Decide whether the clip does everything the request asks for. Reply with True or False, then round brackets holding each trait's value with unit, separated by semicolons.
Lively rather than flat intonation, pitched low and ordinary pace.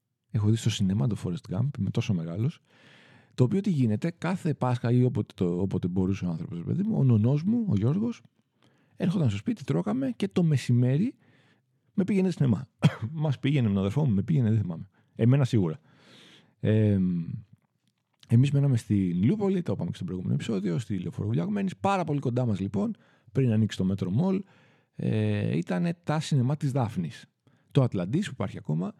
False (7.6 semitones; 130 Hz; 180 wpm)